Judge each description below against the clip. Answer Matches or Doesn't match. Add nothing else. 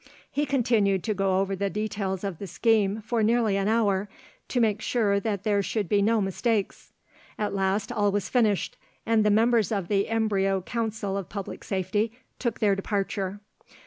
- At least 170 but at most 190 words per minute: Matches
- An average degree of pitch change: Doesn't match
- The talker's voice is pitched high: Matches